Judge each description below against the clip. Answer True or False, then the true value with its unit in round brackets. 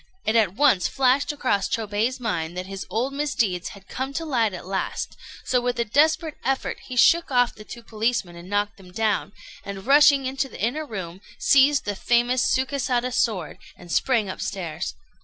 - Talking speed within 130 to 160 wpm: False (180 wpm)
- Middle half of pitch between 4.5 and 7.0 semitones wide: True (5.2 semitones)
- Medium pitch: False (235 Hz)